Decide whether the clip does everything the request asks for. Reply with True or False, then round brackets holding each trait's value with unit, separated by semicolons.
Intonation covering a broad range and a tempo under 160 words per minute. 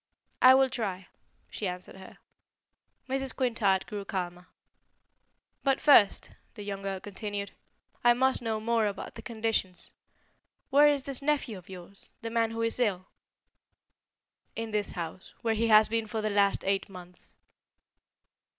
False (3.3 semitones; 150 wpm)